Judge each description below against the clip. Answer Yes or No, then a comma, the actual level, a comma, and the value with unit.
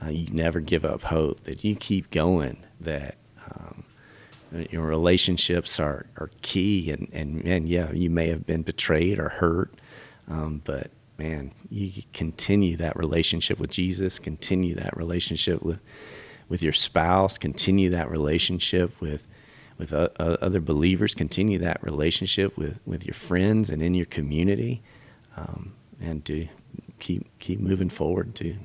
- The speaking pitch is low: Yes, very low, 85 Hz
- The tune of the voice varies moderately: Yes, average, 3.1 semitones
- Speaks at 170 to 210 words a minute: No, average, 150 wpm